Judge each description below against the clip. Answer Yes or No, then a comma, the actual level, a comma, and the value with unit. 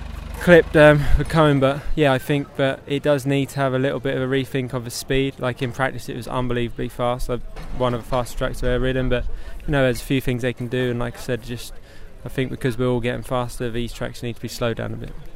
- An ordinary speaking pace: No, fast, 275 wpm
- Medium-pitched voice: No, low, 125 Hz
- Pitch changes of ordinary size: No, narrow, 2.0 semitones